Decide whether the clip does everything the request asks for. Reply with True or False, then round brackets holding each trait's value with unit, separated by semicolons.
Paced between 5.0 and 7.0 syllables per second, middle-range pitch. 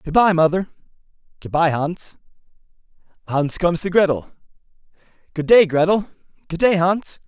True (5.1 syllables/s; 175 Hz)